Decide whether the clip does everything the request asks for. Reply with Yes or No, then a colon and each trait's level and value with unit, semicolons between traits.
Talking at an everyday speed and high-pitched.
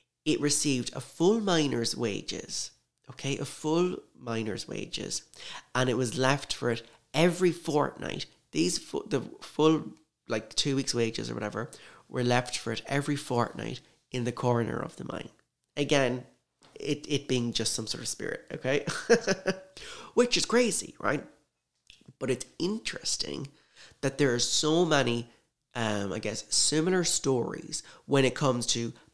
No: average, 150 wpm; low, 135 Hz